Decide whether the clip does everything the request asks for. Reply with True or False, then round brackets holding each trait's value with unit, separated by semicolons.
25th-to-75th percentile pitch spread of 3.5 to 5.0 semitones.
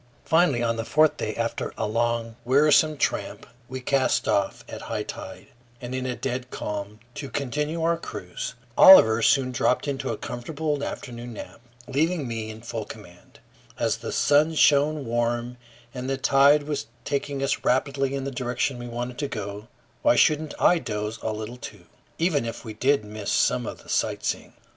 True (3.8 semitones)